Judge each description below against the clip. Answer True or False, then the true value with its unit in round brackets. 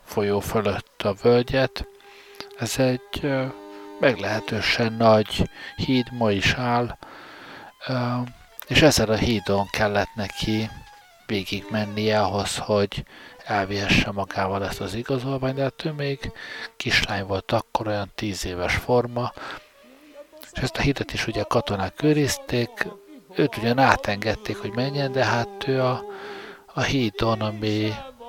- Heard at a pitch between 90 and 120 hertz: True (115 Hz)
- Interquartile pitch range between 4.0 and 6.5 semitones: True (4.4 semitones)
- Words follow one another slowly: False (125 wpm)